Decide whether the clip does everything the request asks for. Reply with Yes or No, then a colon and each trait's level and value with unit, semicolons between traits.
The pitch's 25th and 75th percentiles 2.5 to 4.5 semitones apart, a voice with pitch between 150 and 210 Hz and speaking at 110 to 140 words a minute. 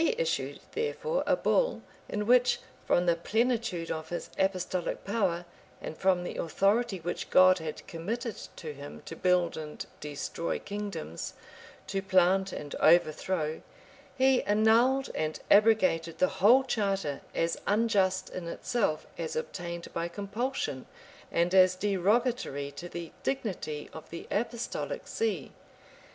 No: average, 5.1 semitones; medium, 185 Hz; slow, 135 wpm